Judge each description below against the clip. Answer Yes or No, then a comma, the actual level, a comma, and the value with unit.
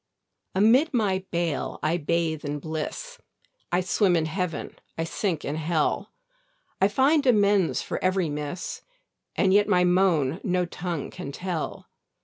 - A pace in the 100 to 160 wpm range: Yes, average, 140 wpm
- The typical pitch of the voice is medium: Yes, medium, 180 Hz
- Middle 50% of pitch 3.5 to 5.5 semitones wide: Yes, average, 3.9 semitones